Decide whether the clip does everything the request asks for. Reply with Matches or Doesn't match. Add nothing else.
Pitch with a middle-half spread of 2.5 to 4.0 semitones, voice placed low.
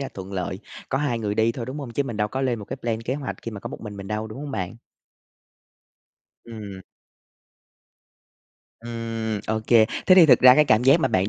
Matches